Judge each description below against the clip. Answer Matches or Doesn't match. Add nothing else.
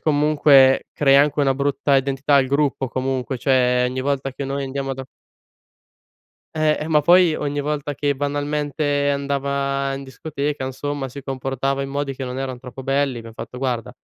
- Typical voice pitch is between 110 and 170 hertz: Matches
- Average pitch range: Doesn't match